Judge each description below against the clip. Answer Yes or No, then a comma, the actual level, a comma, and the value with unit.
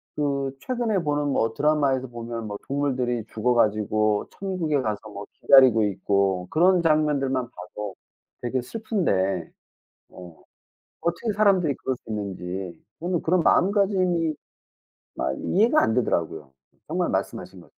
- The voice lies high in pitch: No, low, 130 Hz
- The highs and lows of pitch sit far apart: Yes, wide, 7.9 semitones